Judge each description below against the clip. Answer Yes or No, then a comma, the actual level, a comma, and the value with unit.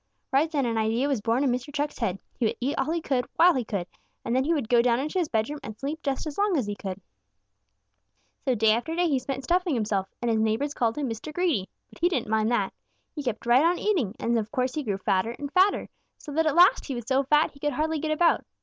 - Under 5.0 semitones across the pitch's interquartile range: No, average, 5.3 semitones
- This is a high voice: Yes, very high, 265 Hz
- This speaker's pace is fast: Yes, fast, 265 wpm